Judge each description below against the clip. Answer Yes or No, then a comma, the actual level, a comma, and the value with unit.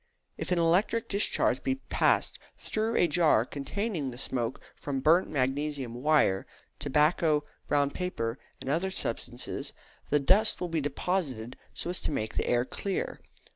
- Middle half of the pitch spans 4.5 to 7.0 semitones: Yes, average, 5.3 semitones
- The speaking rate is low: No, average, 150 wpm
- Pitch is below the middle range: No, medium, 150 Hz